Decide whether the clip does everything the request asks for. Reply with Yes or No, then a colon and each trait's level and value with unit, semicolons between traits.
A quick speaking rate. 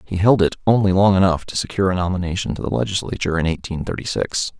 Yes: fast, 220 wpm